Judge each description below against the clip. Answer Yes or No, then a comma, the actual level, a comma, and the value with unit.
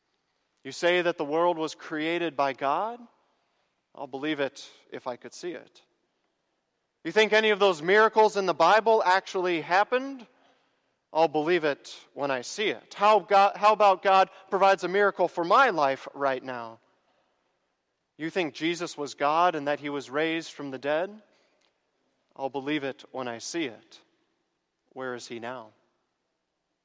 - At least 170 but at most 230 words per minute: No, average, 160 wpm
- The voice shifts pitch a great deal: Yes, wide, 5.8 semitones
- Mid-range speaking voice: Yes, medium, 165 Hz